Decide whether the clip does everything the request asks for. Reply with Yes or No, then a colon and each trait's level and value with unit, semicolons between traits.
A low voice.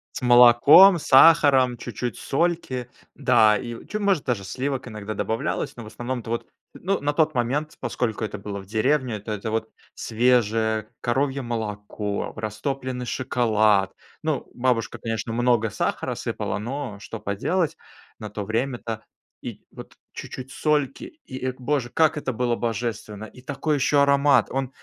Yes: low, 120 Hz